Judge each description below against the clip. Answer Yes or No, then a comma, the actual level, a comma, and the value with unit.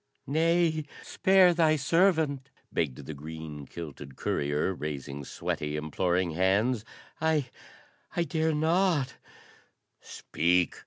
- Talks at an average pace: No, slow, 105 wpm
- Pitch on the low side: Yes, low, 100 Hz